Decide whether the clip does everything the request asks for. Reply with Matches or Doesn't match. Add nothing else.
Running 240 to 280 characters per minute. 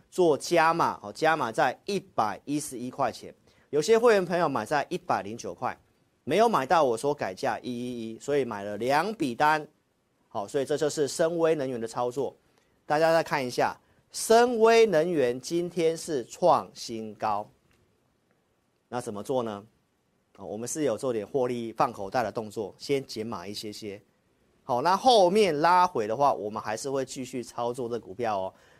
Matches